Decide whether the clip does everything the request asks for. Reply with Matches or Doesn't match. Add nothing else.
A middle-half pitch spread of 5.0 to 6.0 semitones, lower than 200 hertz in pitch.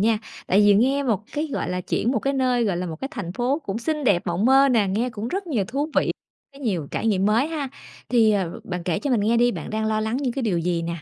Doesn't match